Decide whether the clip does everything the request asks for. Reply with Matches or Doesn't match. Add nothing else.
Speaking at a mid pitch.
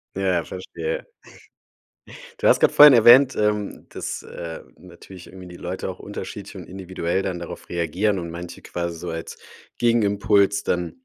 Doesn't match